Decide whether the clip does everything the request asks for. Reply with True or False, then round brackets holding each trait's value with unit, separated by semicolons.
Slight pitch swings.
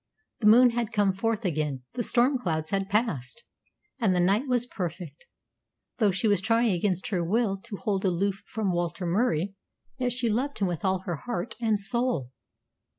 False (4.8 semitones)